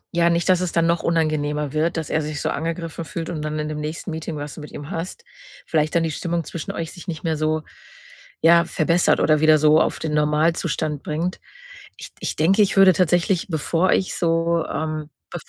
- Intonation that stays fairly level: Yes, narrow, 1.8 semitones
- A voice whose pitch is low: No, medium, 160 Hz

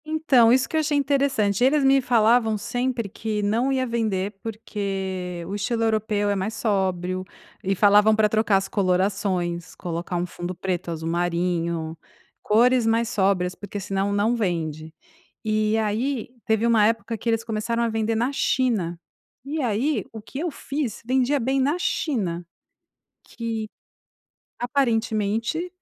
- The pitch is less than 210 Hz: No, high, 220 Hz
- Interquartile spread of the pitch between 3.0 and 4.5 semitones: Yes, average, 4.0 semitones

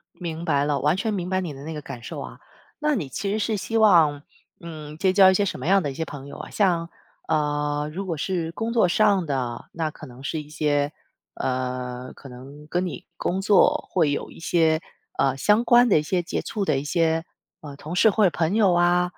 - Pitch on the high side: No, medium, 165 Hz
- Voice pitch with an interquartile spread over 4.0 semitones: Yes, average, 4.4 semitones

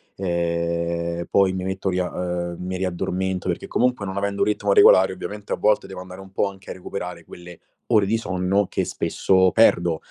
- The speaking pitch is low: Yes, very low, 95 Hz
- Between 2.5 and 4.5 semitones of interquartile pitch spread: No, narrow, 2.0 semitones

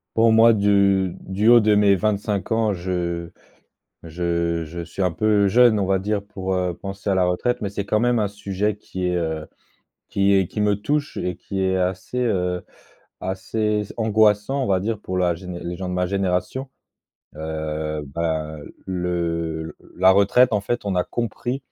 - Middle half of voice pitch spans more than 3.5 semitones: No, average, 3.0 semitones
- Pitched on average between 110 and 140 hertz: No, very low, 95 Hz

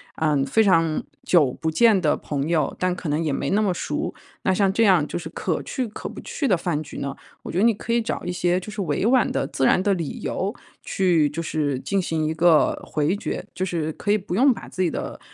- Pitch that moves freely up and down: No, average, 4.4 semitones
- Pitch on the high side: No, medium, 175 Hz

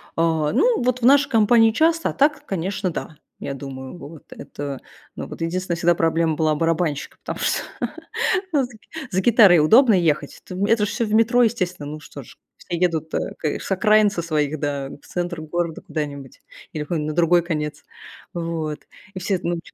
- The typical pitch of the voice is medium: Yes, medium, 170 Hz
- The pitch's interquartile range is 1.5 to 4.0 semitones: No, wide, 5.4 semitones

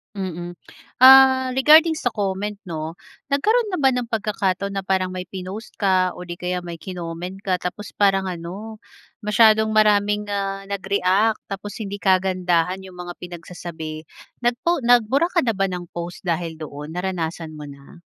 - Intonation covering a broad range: No, average, 3.5 semitones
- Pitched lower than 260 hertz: Yes, high, 190 Hz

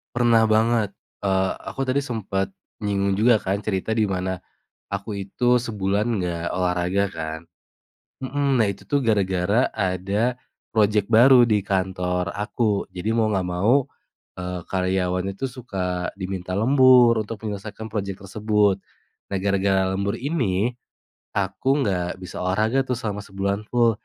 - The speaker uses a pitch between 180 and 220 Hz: No, low, 100 Hz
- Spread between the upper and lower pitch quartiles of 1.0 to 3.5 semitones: Yes, average, 3.2 semitones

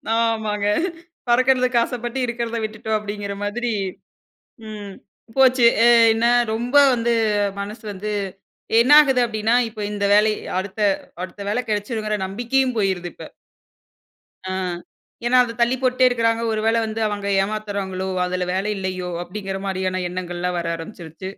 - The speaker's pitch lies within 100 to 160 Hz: No, high, 215 Hz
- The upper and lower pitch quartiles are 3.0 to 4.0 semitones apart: Yes, average, 3.4 semitones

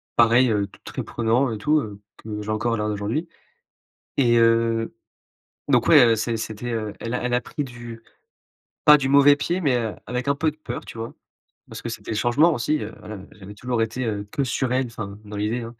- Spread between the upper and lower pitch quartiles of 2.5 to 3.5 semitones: Yes, average, 3.0 semitones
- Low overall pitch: Yes, low, 115 Hz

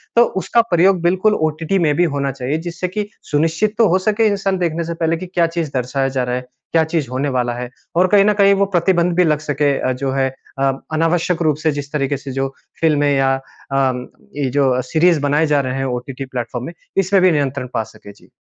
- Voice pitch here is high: No, medium, 150 Hz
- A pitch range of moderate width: Yes, average, 4.7 semitones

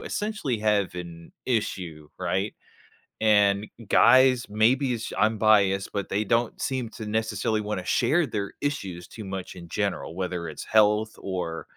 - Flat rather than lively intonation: No, average, 3.1 semitones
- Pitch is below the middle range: Yes, low, 105 Hz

